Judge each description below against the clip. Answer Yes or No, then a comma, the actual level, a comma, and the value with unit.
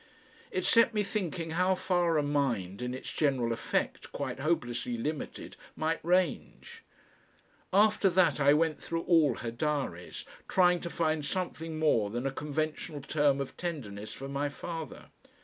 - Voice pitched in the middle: Yes, medium, 155 Hz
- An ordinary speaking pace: Yes, average, 150 wpm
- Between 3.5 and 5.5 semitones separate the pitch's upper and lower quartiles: Yes, average, 4.4 semitones